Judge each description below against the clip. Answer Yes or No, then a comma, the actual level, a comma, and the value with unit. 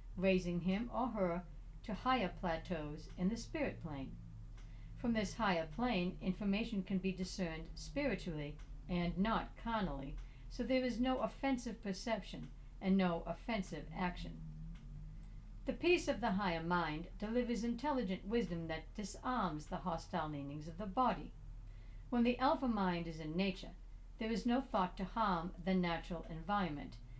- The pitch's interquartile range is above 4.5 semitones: Yes, wide, 5.5 semitones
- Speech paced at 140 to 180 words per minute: Yes, average, 145 wpm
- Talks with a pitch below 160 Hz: No, medium, 185 Hz